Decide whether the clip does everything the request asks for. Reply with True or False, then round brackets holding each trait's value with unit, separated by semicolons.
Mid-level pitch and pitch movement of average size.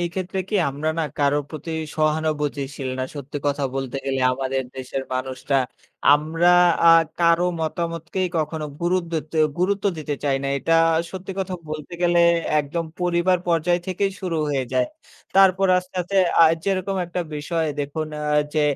True (160 Hz; 3.7 semitones)